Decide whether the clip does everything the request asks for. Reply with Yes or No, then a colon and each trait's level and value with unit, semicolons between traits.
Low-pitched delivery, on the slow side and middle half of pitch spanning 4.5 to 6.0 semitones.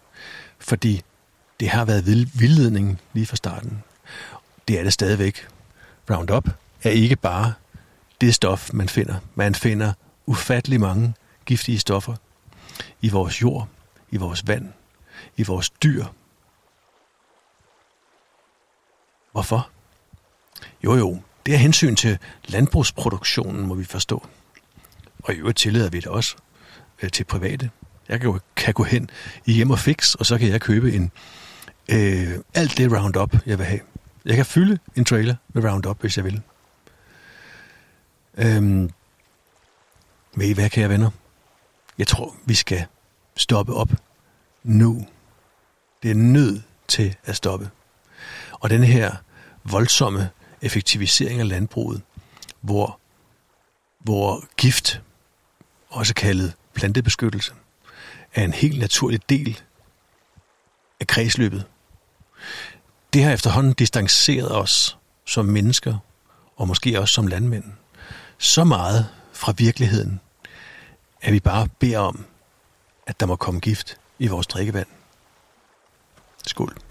No: low, 110 Hz; slow, 120 wpm; average, 3.2 semitones